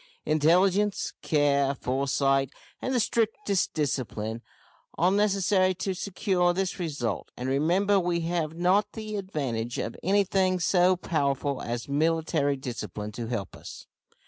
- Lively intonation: Yes, wide, 5.7 semitones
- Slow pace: Yes, slow, 125 wpm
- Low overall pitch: No, medium, 165 Hz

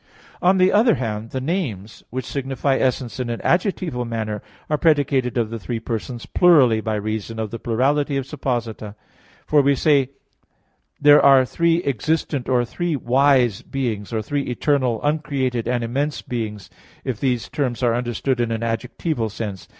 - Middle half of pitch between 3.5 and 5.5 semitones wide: Yes, average, 3.9 semitones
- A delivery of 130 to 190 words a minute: Yes, average, 165 wpm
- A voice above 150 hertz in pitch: No, low, 125 Hz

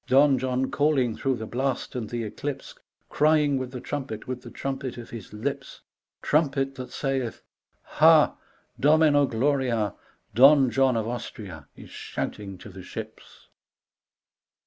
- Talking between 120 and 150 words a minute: Yes, average, 145 wpm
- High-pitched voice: No, low, 130 Hz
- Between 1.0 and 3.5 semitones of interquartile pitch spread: Yes, average, 3.2 semitones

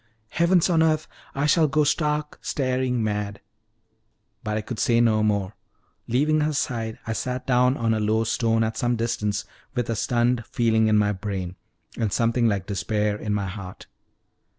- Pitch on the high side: No, low, 115 Hz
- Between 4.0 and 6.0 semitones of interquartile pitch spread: No, average, 3.5 semitones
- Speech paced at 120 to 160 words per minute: No, average, 175 wpm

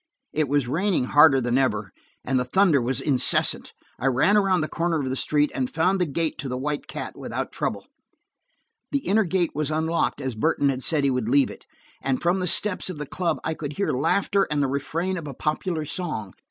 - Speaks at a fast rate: Yes, fast, 220 wpm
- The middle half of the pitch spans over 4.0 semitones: Yes, average, 4.5 semitones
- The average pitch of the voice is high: No, medium, 150 Hz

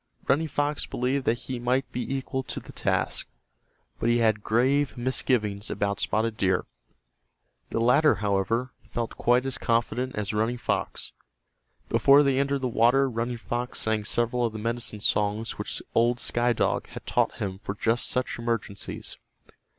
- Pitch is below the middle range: Yes, low, 120 Hz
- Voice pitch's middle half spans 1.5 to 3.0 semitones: Yes, average, 2.7 semitones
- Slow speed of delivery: No, average, 160 wpm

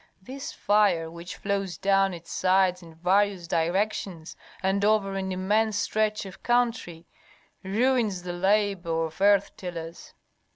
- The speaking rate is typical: No, slow, 130 wpm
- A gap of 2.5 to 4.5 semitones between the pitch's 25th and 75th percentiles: Yes, average, 2.9 semitones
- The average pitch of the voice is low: No, high, 195 Hz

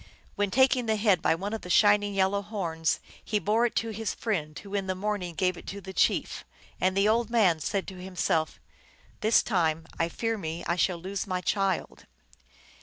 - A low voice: No, high, 195 Hz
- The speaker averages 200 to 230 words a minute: Yes, fast, 205 wpm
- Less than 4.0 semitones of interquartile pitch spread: Yes, average, 2.9 semitones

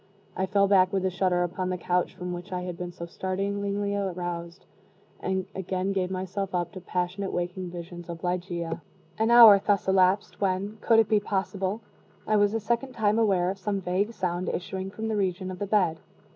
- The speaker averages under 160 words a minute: No, average, 200 wpm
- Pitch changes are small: Yes, narrow, 2.1 semitones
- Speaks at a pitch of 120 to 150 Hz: No, high, 190 Hz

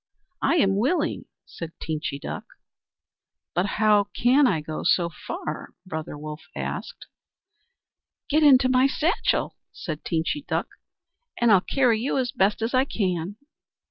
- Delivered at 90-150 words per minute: Yes, slow, 135 wpm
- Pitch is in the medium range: No, high, 205 Hz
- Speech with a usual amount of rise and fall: No, wide, 7.8 semitones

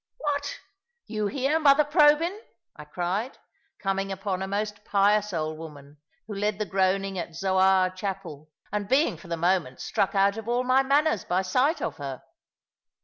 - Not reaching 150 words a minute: No, average, 165 wpm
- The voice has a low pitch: No, high, 195 Hz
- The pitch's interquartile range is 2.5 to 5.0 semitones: No, wide, 5.5 semitones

